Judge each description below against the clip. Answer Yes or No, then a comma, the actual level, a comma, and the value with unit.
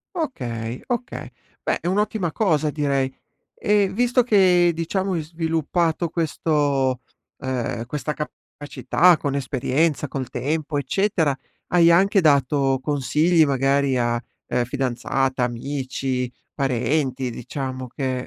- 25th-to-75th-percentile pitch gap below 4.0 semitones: No, average, 4.4 semitones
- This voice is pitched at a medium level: Yes, medium, 145 Hz